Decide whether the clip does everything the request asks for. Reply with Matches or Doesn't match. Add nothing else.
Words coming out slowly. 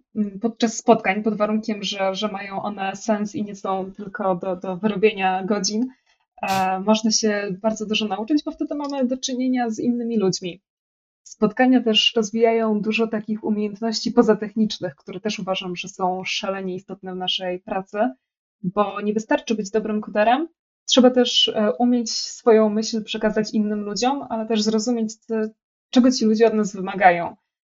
Doesn't match